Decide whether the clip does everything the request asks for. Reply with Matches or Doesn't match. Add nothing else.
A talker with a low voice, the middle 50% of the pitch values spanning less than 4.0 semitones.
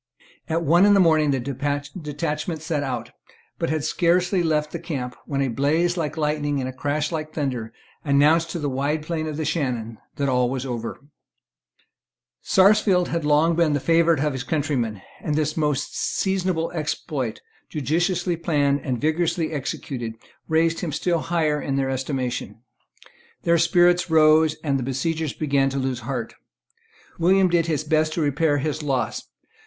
Doesn't match